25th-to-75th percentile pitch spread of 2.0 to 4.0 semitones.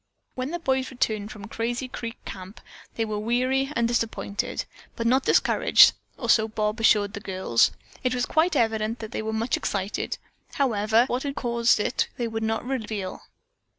Yes: average, 2.8 semitones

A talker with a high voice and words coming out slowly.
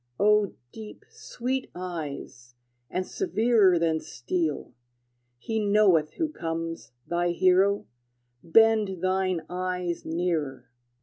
No: medium, 180 Hz; slow, 100 wpm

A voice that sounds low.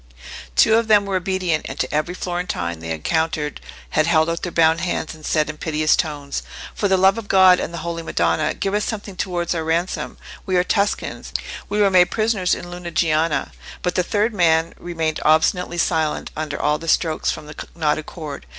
No: medium, 170 Hz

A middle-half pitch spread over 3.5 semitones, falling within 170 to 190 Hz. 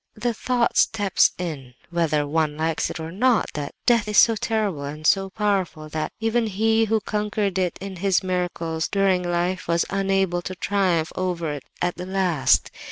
Yes: average, 4.0 semitones; medium, 185 Hz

